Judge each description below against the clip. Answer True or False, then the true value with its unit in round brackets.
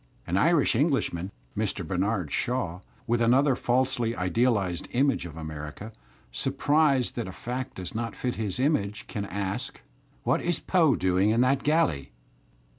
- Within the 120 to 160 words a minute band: True (145 wpm)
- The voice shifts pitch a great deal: True (6.1 semitones)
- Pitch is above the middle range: False (115 Hz)